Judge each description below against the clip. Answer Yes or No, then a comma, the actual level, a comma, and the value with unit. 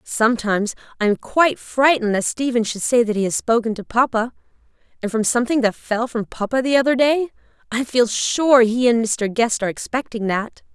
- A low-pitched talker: No, high, 235 Hz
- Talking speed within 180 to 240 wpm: Yes, average, 195 wpm